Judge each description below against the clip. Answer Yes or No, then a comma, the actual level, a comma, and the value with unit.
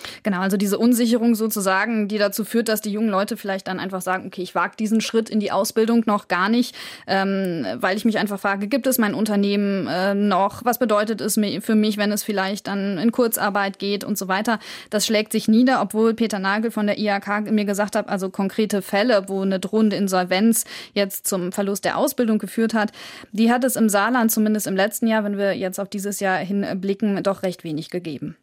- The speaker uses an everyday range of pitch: No, narrow, 2.0 semitones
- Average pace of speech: No, fast, 215 wpm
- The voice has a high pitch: Yes, high, 205 Hz